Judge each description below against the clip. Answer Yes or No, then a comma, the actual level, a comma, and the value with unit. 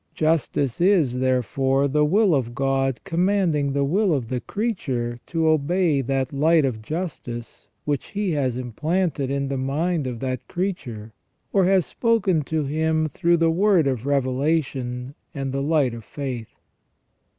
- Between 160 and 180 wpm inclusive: No, average, 150 wpm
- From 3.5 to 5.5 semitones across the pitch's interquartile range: Yes, average, 4.4 semitones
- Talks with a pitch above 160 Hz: No, medium, 140 Hz